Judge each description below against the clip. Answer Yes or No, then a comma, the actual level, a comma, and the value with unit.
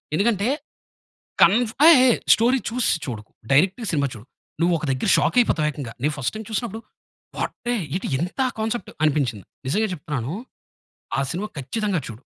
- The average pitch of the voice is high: No, medium, 175 Hz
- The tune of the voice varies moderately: No, wide, 8.0 semitones